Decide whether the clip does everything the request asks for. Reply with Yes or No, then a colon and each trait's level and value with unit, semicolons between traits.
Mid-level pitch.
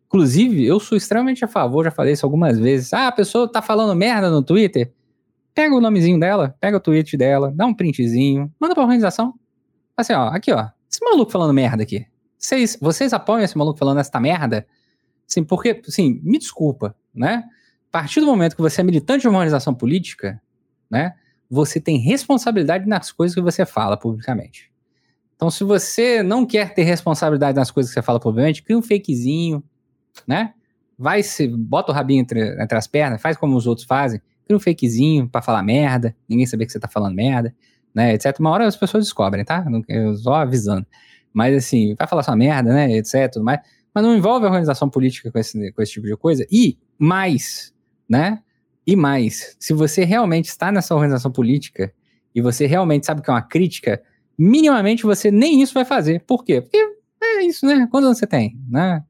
Yes: medium, 155 Hz